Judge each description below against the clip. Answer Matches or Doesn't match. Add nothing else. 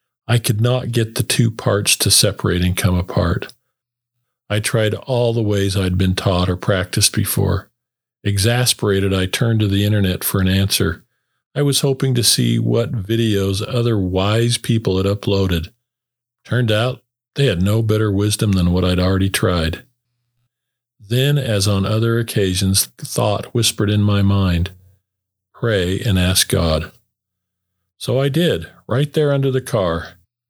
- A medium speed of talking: Matches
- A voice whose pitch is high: Doesn't match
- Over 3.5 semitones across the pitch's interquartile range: Matches